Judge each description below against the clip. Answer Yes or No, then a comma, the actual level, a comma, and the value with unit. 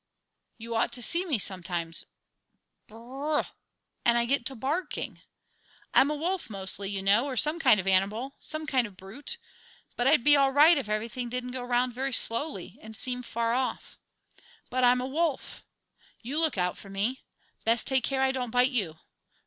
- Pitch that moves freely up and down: No, average, 4.0 semitones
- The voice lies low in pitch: No, very high, 250 Hz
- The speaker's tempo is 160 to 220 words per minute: Yes, average, 200 wpm